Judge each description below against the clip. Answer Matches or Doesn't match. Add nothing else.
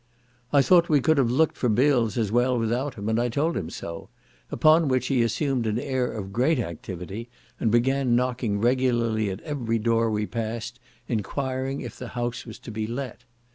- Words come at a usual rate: Matches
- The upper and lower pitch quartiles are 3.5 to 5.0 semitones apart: Doesn't match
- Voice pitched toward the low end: Matches